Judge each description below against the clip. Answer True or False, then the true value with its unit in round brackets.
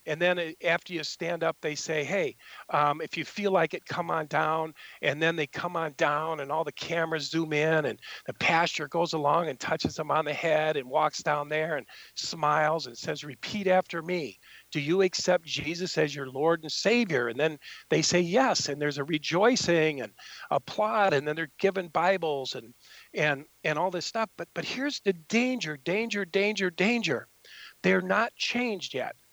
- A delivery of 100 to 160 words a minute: False (195 wpm)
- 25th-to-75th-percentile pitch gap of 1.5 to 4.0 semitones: True (3.3 semitones)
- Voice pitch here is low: False (165 Hz)